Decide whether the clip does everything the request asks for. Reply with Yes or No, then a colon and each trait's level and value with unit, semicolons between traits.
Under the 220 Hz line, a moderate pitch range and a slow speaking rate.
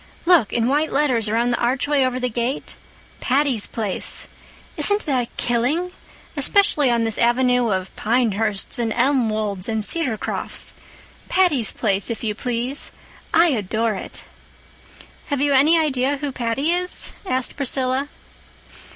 No: very high, 250 Hz; average, 4.0 semitones; slow, 130 wpm